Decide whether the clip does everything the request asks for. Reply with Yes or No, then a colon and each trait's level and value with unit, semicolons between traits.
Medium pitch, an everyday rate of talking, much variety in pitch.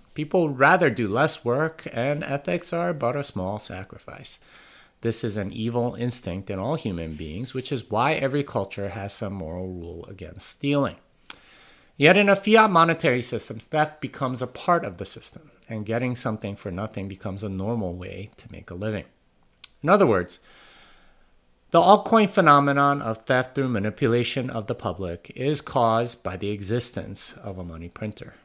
No: low, 115 Hz; average, 170 wpm; wide, 6.1 semitones